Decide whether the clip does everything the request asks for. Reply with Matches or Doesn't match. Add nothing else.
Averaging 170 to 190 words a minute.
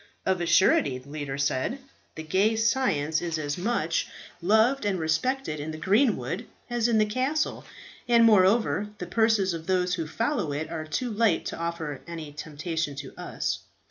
Matches